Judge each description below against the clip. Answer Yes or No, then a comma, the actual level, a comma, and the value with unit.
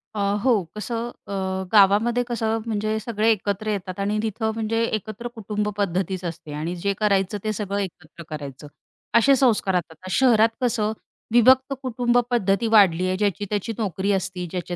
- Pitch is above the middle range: Yes, high, 210 Hz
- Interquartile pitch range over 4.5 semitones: No, average, 3.2 semitones